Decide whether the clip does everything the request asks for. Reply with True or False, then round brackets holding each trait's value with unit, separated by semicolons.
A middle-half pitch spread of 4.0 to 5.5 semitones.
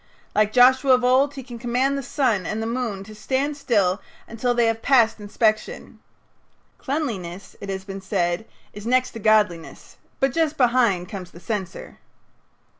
True (4.5 semitones)